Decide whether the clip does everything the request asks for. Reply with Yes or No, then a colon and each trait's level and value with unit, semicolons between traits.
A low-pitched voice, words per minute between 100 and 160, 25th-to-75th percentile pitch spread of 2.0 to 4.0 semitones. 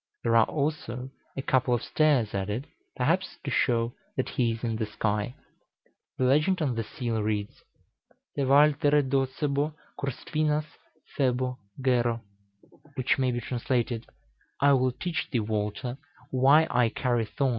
Yes: low, 130 Hz; average, 155 wpm; average, 3.4 semitones